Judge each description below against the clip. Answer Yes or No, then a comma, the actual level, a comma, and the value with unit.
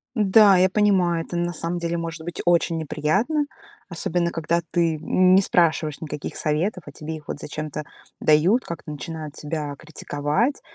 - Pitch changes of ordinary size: Yes, average, 3.0 semitones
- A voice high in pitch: No, medium, 170 Hz